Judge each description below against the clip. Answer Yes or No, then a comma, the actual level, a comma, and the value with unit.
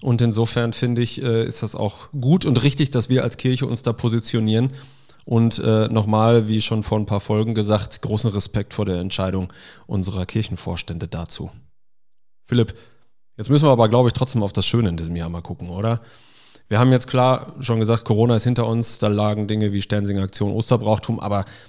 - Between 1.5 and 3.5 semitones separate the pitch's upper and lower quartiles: Yes, narrow, 2.5 semitones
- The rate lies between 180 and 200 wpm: Yes, fast, 190 wpm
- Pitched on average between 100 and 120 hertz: Yes, low, 115 Hz